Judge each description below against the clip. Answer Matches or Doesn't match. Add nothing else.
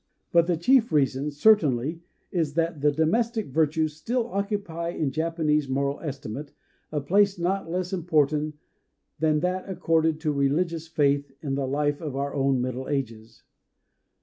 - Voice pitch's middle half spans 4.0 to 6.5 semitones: Doesn't match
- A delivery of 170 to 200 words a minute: Doesn't match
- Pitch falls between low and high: Matches